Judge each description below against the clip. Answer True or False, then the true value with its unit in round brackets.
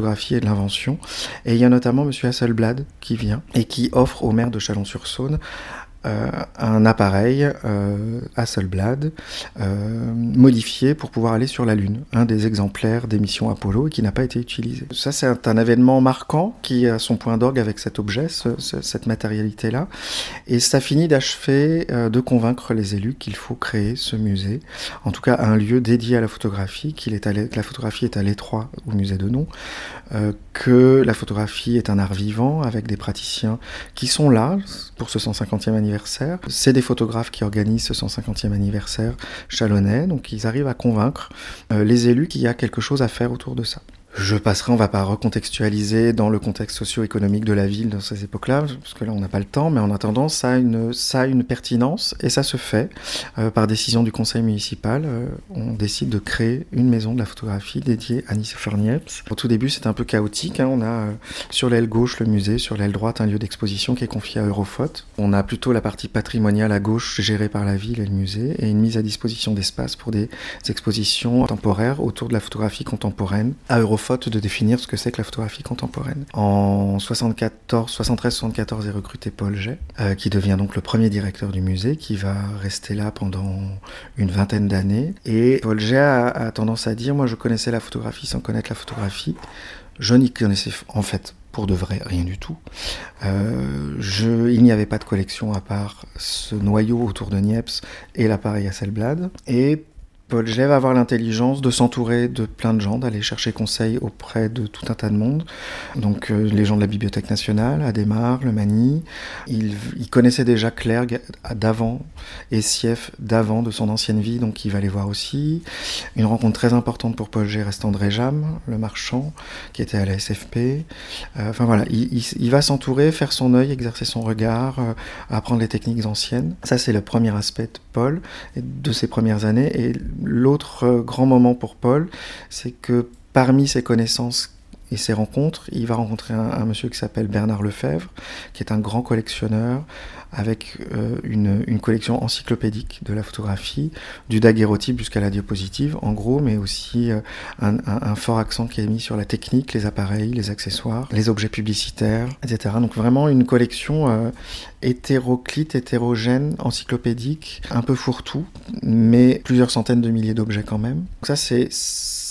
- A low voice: True (115 Hz)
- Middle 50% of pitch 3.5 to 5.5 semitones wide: False (2.7 semitones)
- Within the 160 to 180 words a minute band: False (195 wpm)